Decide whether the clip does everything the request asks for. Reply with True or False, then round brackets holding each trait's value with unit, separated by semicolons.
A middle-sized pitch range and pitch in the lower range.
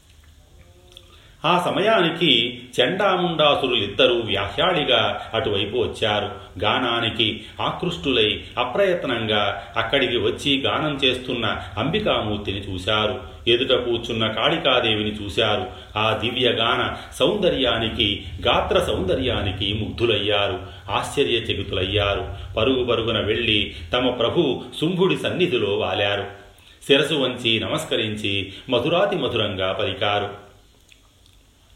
True (3.7 semitones; 105 Hz)